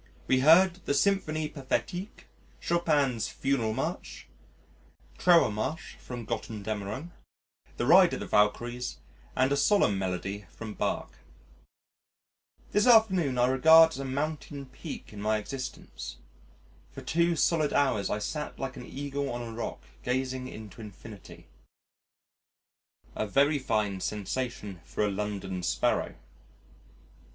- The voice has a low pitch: Yes, low, 130 Hz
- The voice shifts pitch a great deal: Yes, wide, 6.2 semitones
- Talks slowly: Yes, slow, 125 wpm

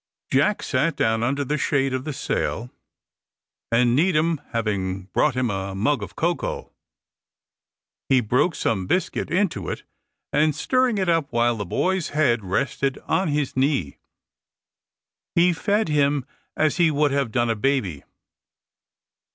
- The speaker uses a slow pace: No, average, 145 wpm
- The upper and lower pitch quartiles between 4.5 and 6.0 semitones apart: Yes, average, 5.2 semitones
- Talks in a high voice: No, medium, 140 Hz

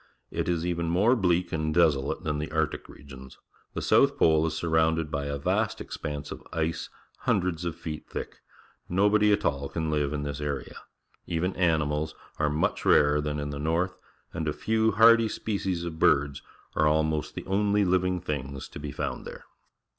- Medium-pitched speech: No, very low, 80 Hz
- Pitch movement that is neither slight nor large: Yes, average, 3.3 semitones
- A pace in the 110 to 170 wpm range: No, average, 180 wpm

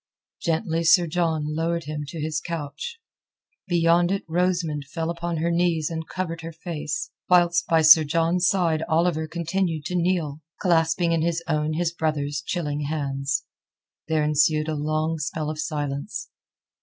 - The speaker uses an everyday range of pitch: No, narrow, 2.0 semitones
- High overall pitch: No, medium, 165 Hz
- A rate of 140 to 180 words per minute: Yes, average, 155 wpm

